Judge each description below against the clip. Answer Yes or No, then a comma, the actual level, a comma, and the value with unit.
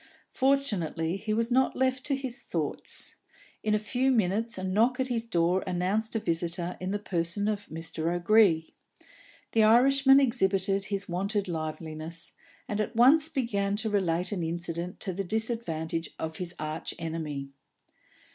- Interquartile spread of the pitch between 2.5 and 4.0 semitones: No, average, 5.3 semitones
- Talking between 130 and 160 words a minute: Yes, average, 150 wpm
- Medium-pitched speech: No, high, 200 Hz